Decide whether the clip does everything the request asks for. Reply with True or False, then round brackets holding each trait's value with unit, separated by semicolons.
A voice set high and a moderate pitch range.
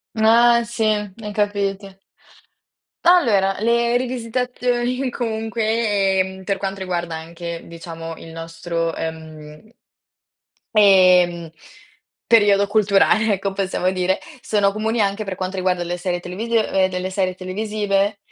True (195 Hz; 3.3 semitones)